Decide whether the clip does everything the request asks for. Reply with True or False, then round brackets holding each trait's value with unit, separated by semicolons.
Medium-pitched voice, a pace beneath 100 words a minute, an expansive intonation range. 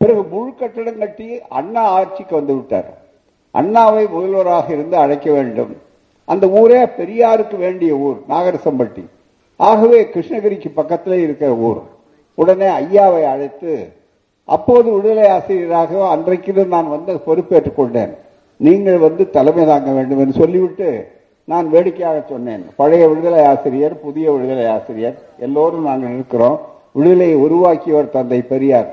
False (175 Hz; 120 wpm; 5.8 semitones)